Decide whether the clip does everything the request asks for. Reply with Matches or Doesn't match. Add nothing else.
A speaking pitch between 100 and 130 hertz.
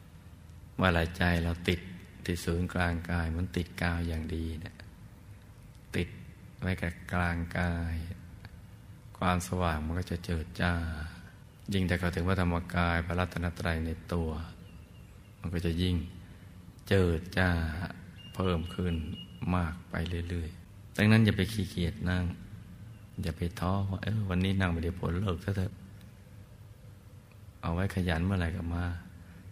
Doesn't match